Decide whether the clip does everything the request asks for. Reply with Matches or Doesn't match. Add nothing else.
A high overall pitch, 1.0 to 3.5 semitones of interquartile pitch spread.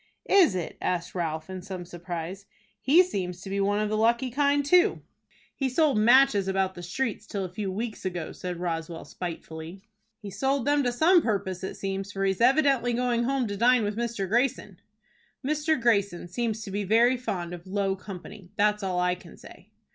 Doesn't match